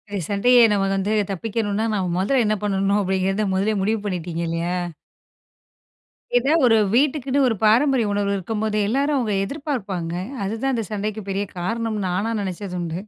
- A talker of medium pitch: No, high, 210 Hz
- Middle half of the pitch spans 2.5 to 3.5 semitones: Yes, average, 3.1 semitones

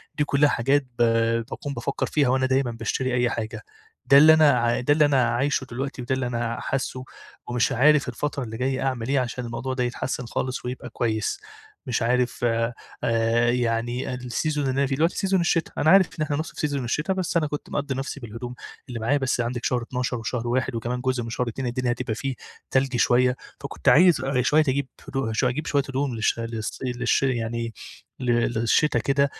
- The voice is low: Yes, low, 125 Hz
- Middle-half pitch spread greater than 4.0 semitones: No, average, 2.7 semitones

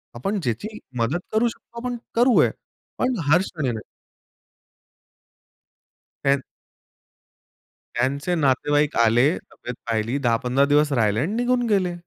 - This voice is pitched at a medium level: Yes, medium, 145 Hz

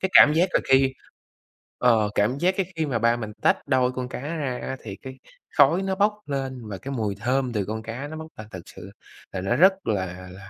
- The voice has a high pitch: No, low, 125 Hz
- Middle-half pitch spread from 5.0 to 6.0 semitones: Yes, average, 5.3 semitones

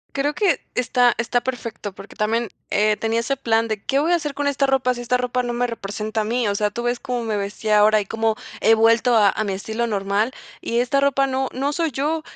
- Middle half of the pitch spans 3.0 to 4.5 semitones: Yes, average, 3.3 semitones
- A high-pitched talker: Yes, high, 235 Hz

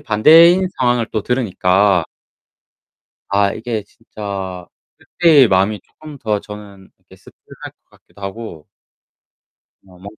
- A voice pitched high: No, low, 105 Hz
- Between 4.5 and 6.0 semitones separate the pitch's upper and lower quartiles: No, average, 4.0 semitones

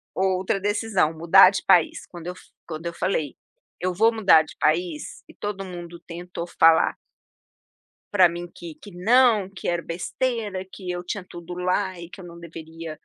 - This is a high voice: No, medium, 180 Hz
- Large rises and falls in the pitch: No, narrow, 2.4 semitones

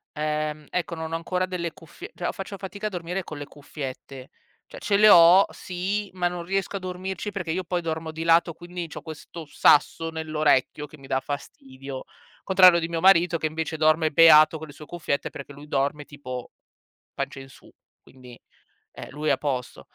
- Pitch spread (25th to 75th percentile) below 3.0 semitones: No, average, 3.4 semitones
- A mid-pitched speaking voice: Yes, medium, 160 Hz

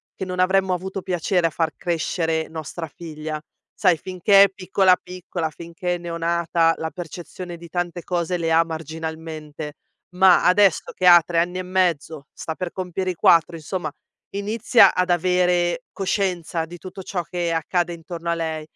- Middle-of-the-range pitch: Yes, medium, 175 Hz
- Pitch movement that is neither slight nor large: No, narrow, 2.0 semitones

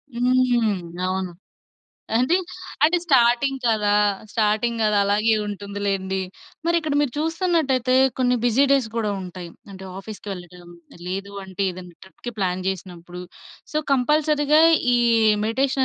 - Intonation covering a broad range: Yes, wide, 5.7 semitones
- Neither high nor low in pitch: No, high, 220 Hz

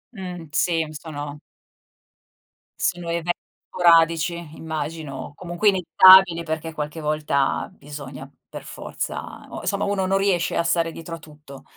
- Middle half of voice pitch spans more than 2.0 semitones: Yes, narrow, 2.6 semitones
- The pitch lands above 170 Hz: No, medium, 165 Hz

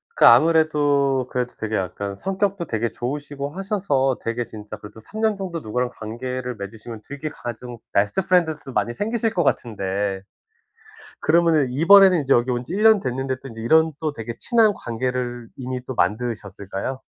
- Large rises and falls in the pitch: Yes, wide, 5.8 semitones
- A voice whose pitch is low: Yes, low, 130 Hz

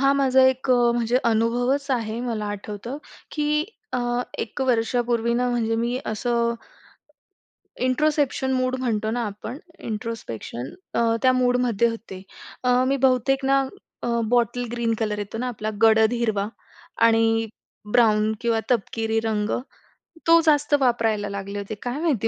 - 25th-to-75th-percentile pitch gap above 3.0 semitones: No, narrow, 2.4 semitones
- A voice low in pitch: No, high, 235 Hz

